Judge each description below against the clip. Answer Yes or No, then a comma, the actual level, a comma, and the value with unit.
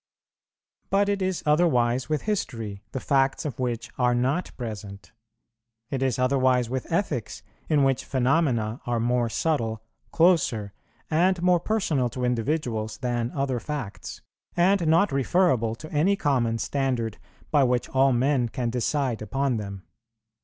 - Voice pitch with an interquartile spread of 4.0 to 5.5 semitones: Yes, average, 4.6 semitones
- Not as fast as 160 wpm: Yes, average, 140 wpm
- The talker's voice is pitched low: Yes, low, 130 Hz